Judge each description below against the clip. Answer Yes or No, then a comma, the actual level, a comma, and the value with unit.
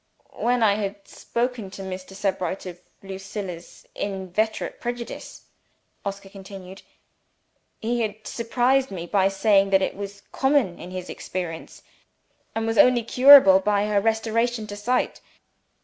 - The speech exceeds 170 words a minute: No, slow, 135 wpm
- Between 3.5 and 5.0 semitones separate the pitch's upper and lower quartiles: No, average, 3.1 semitones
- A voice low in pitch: No, high, 200 Hz